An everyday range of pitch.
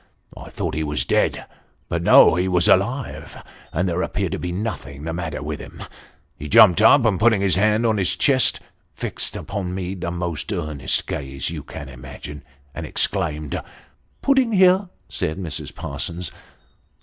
No: wide, 5.7 semitones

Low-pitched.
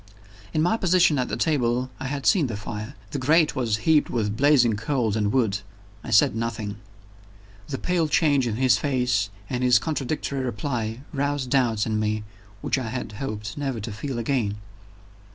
Yes: low, 125 Hz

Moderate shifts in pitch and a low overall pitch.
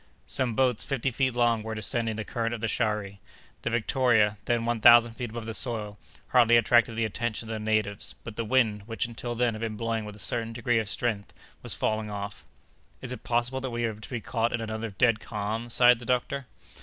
No: narrow, 1.8 semitones; low, 115 Hz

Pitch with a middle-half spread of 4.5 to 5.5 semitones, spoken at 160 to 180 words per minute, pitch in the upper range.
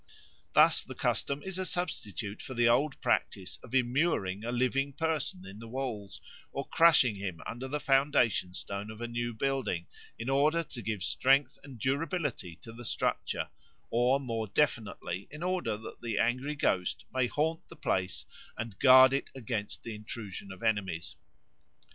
No: average, 4.8 semitones; average, 165 wpm; low, 120 Hz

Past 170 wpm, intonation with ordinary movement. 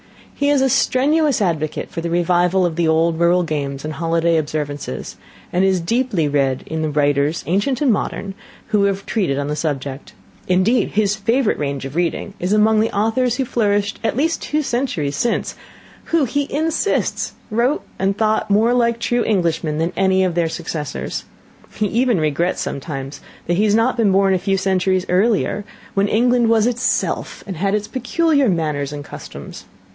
No: average, 180 wpm; wide, 6.2 semitones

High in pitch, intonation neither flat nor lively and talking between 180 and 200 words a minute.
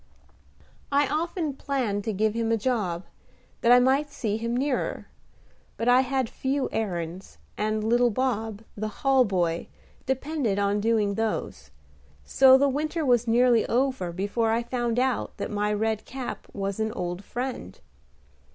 No: high, 230 Hz; average, 4.1 semitones; average, 150 wpm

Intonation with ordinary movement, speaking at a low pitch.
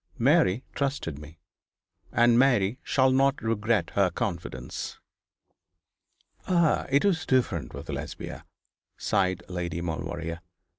No: wide, 7.5 semitones; low, 115 Hz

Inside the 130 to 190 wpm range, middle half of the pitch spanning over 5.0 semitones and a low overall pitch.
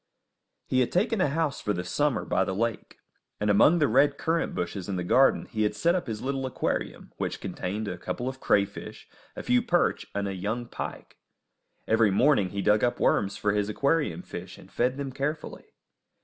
No: average, 200 wpm; wide, 5.6 semitones; low, 115 Hz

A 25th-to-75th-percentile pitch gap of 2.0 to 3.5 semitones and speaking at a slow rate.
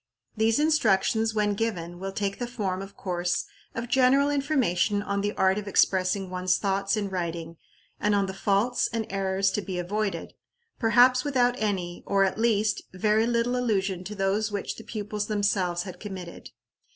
No: average, 2.9 semitones; average, 170 wpm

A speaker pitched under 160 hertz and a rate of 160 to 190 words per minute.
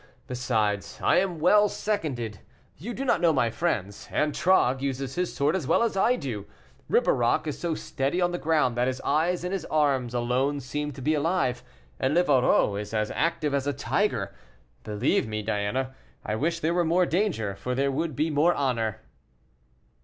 Yes: medium, 140 Hz; average, 185 wpm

